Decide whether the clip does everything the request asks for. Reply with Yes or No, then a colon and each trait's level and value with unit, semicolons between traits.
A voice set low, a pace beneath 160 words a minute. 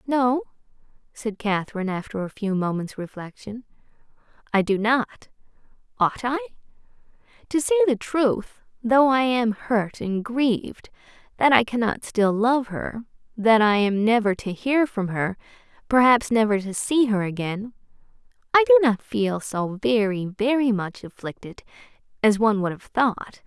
No: high, 220 Hz; average, 145 wpm